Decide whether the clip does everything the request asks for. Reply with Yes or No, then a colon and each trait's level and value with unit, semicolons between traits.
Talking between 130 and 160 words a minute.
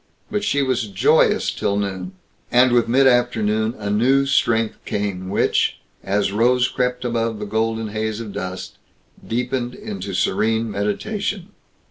Yes: average, 140 wpm